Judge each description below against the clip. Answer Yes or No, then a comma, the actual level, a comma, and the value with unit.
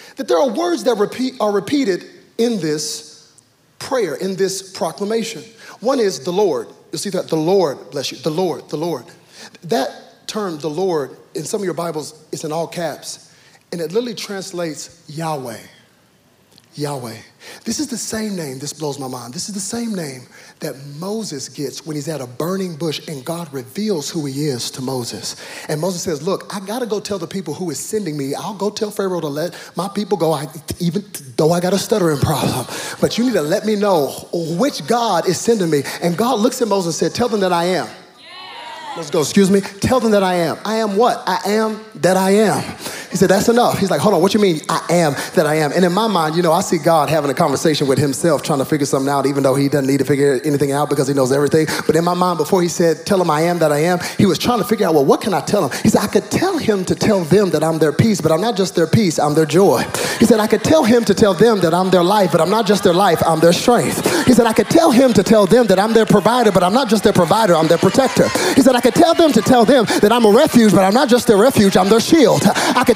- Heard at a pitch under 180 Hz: No, medium, 185 Hz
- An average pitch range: No, wide, 5.7 semitones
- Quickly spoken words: Yes, fast, 260 wpm